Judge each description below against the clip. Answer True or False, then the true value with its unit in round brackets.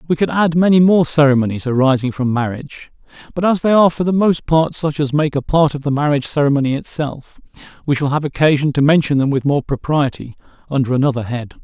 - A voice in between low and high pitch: True (145 Hz)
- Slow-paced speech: False (205 wpm)